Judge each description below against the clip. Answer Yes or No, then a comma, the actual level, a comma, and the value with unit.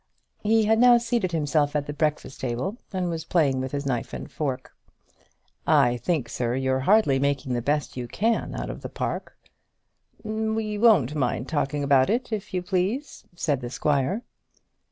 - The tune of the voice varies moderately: No, wide, 7.9 semitones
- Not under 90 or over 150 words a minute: No, average, 175 wpm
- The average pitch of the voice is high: No, medium, 150 Hz